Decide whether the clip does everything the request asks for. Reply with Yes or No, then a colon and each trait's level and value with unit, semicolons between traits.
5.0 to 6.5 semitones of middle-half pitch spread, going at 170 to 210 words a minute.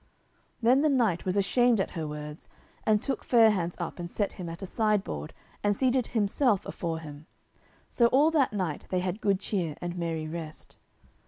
Yes: wide, 5.4 semitones; average, 185 wpm